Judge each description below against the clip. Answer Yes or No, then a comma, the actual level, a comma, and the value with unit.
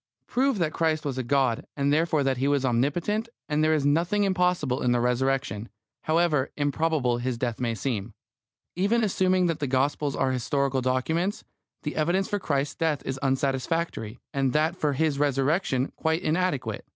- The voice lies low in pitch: No, medium, 145 Hz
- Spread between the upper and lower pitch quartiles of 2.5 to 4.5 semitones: Yes, average, 4.1 semitones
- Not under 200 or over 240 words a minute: No, average, 165 wpm